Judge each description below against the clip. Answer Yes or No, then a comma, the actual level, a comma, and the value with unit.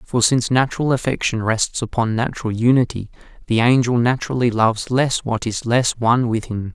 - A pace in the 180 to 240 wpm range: No, average, 170 wpm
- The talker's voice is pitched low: Yes, low, 120 Hz